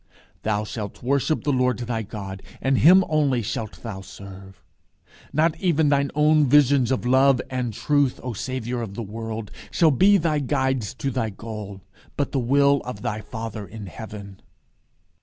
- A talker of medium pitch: No, low, 125 Hz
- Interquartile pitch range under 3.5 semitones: No, average, 4.7 semitones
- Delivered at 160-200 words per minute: Yes, average, 165 wpm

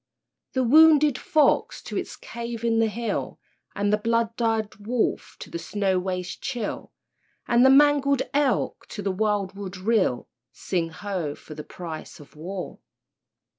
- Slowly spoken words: No, average, 155 wpm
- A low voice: No, high, 215 Hz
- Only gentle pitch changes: No, average, 4.7 semitones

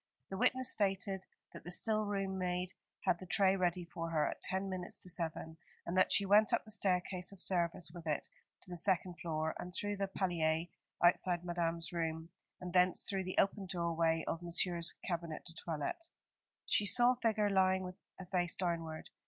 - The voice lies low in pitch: No, medium, 180 Hz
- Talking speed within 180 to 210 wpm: Yes, average, 190 wpm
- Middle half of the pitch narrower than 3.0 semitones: Yes, narrow, 2.4 semitones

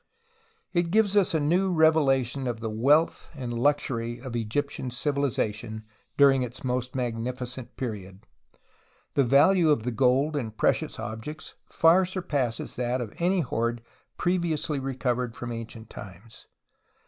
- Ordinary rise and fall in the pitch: Yes, average, 4.4 semitones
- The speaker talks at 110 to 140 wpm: Yes, slow, 135 wpm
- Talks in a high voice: No, low, 130 Hz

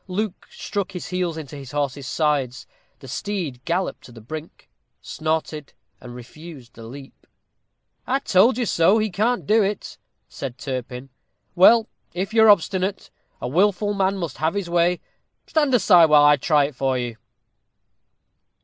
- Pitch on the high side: No, medium, 165 Hz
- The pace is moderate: Yes, average, 160 wpm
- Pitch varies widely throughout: Yes, wide, 6.3 semitones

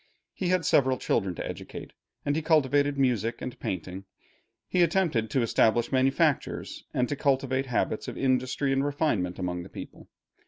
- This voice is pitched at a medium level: No, low, 130 Hz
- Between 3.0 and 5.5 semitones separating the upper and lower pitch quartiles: Yes, average, 4.0 semitones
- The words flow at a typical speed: Yes, average, 160 wpm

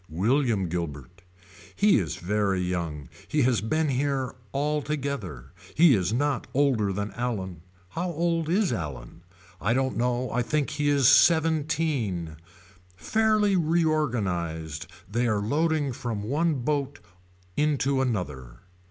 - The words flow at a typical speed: No, slow, 125 wpm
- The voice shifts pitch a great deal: Yes, wide, 8.2 semitones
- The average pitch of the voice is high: No, low, 125 Hz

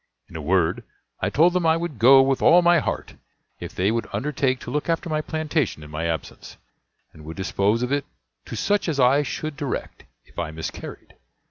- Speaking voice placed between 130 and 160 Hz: Yes, low, 135 Hz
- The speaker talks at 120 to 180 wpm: No, fast, 205 wpm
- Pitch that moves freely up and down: Yes, wide, 8.5 semitones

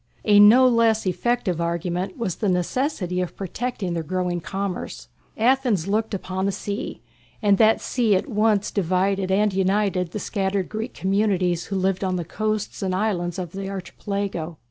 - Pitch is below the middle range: No, high, 195 Hz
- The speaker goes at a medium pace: Yes, average, 165 wpm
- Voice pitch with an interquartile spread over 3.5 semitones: No, average, 2.8 semitones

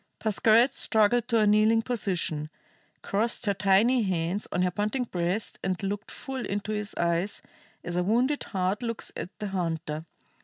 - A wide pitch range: No, average, 3.7 semitones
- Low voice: No, high, 205 Hz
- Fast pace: No, average, 160 wpm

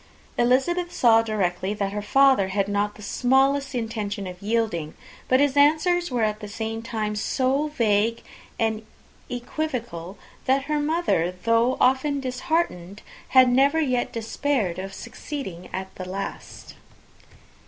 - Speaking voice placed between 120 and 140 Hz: No, high, 230 Hz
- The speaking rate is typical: No, slow, 130 wpm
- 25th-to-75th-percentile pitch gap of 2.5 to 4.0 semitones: No, average, 5.0 semitones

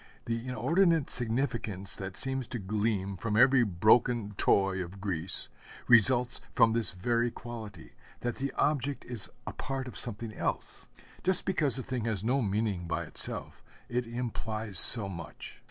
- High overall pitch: No, low, 115 Hz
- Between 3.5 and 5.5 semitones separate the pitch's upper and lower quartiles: Yes, average, 4.1 semitones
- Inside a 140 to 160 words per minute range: Yes, average, 155 wpm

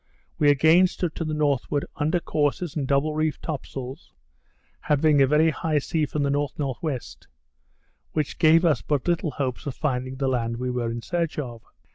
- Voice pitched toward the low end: No, medium, 145 Hz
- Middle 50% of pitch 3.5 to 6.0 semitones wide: No, average, 2.9 semitones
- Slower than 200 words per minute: Yes, average, 180 wpm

